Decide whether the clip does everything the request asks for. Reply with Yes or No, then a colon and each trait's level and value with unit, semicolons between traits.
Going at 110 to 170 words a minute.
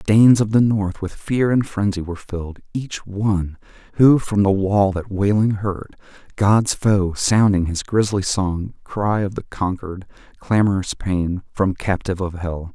Yes: average, 165 wpm